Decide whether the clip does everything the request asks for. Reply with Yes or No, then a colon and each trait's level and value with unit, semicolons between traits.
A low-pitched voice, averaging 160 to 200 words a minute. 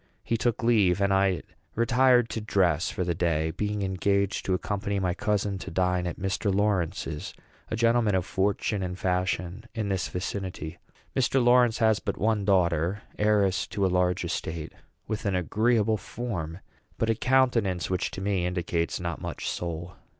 Yes: very low, 95 Hz; average, 165 wpm